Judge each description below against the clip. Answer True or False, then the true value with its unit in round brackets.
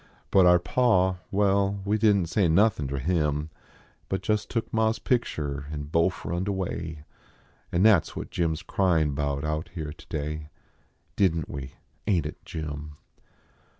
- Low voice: True (85 Hz)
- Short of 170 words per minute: False (175 wpm)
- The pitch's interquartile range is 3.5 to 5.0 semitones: True (4.7 semitones)